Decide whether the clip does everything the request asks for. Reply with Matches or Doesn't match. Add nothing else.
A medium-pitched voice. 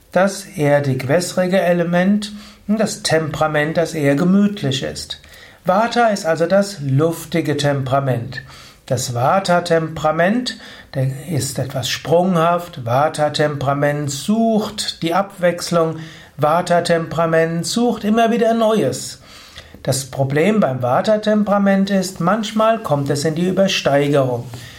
Matches